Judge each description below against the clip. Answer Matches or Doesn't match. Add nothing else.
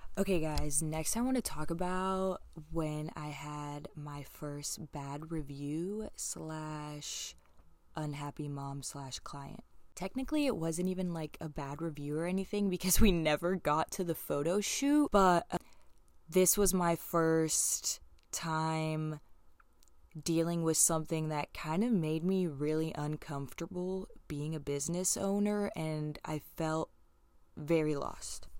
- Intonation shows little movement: Doesn't match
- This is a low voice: Doesn't match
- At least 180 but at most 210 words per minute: Doesn't match